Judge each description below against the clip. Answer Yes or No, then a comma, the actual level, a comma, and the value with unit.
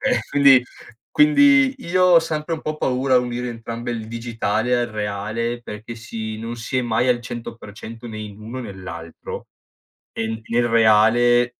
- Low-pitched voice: Yes, low, 120 Hz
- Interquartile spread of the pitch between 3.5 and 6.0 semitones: No, narrow, 2.4 semitones